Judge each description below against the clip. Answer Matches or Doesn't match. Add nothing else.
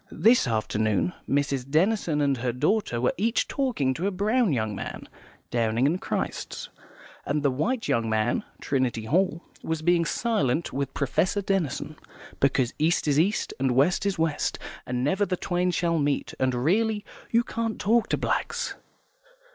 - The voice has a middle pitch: Matches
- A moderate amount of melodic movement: Doesn't match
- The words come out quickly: Doesn't match